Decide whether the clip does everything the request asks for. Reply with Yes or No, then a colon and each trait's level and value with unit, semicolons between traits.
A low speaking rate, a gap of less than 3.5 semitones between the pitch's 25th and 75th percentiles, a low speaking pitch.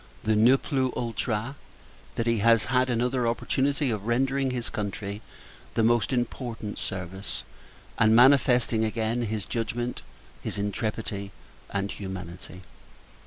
Yes: slow, 120 wpm; average, 3.0 semitones; low, 115 Hz